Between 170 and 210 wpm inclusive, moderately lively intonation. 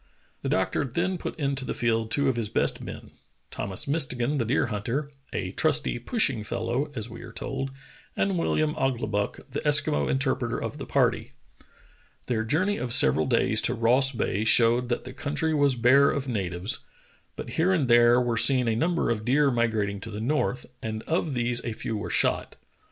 Yes: average, 190 wpm; average, 4.0 semitones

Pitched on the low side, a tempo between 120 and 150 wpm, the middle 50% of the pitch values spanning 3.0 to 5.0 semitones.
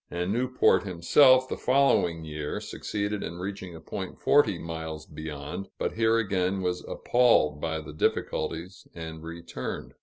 Yes: very low, 90 Hz; average, 145 wpm; average, 4.7 semitones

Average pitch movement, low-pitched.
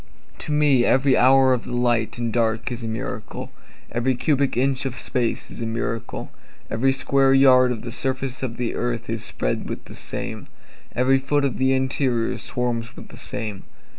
No: narrow, 2.3 semitones; low, 125 Hz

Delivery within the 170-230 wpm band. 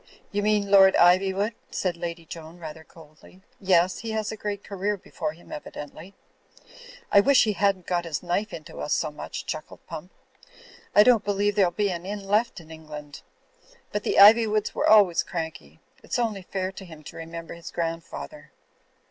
Yes: average, 180 wpm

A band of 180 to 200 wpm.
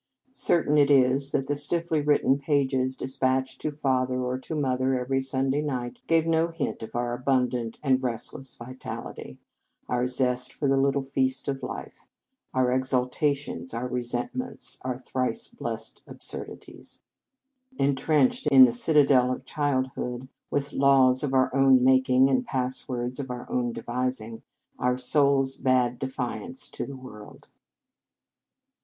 No: average, 145 wpm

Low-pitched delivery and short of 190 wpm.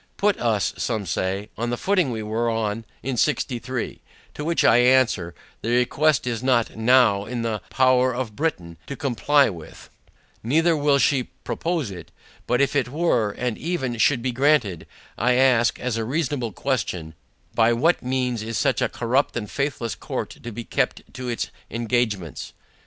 Yes: low, 120 Hz; average, 175 wpm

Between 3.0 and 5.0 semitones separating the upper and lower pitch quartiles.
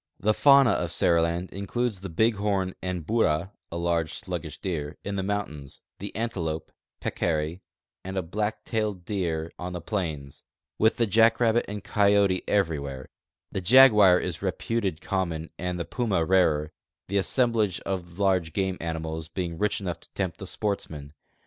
Yes: average, 3.8 semitones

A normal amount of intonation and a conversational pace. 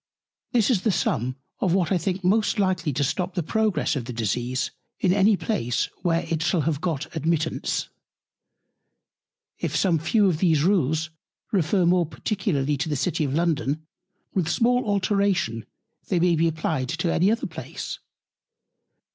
Yes: average, 4.1 semitones; average, 160 wpm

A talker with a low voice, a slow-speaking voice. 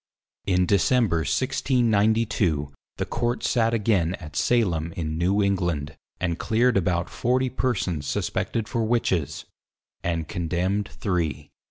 Yes: very low, 95 Hz; slow, 120 wpm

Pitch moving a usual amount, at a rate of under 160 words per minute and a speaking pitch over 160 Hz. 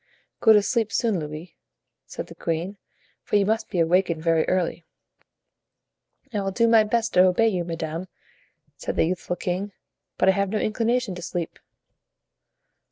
No: average, 4.0 semitones; average, 165 wpm; medium, 185 Hz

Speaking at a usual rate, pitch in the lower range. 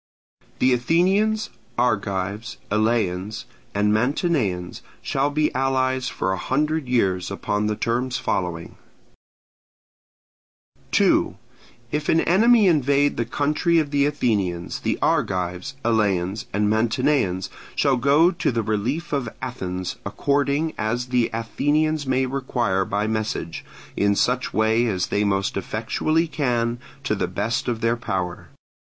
No: slow, 125 wpm; low, 120 Hz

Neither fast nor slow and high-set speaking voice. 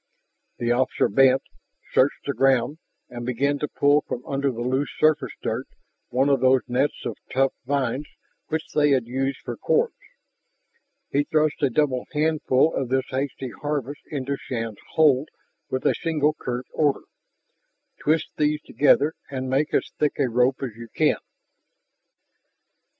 No: average, 150 wpm; low, 135 Hz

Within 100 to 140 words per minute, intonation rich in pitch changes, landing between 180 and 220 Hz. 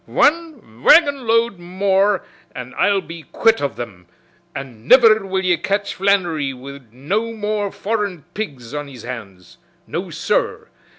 Yes: slow, 135 wpm; wide, 8.1 semitones; high, 190 Hz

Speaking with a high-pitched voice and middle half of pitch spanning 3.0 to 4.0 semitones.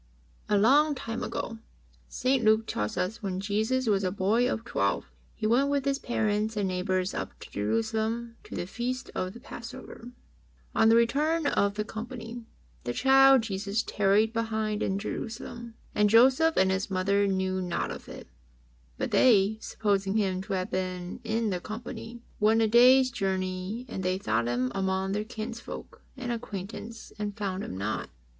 Yes: high, 215 Hz; average, 3.6 semitones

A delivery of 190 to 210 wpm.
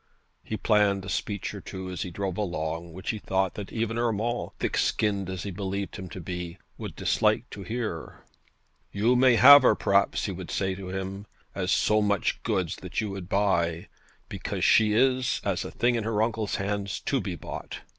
Yes: average, 195 wpm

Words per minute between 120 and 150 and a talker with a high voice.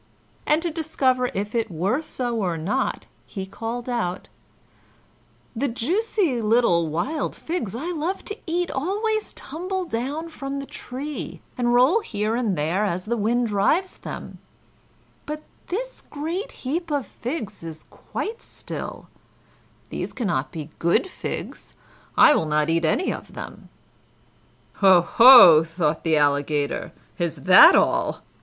Yes: average, 140 wpm; high, 240 Hz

